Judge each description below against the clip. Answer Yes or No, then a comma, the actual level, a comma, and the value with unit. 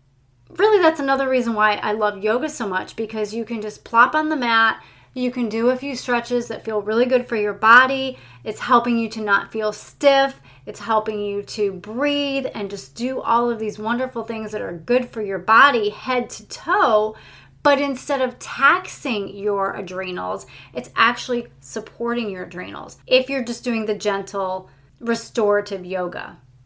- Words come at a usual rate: Yes, average, 180 wpm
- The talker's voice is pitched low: No, high, 225 Hz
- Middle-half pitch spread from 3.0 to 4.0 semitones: Yes, average, 3.6 semitones